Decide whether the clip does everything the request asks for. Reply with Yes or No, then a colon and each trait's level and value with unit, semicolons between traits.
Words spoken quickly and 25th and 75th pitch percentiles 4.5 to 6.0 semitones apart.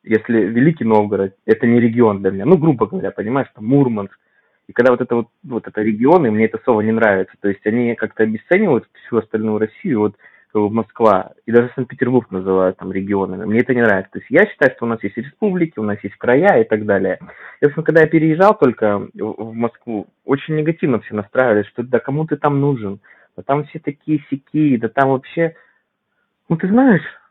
Yes: fast, 200 wpm; average, 5.1 semitones